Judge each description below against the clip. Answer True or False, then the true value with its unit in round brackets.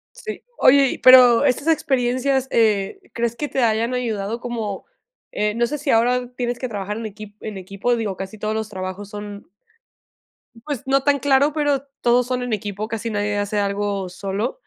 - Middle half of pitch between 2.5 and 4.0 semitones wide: True (3.7 semitones)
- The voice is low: False (230 Hz)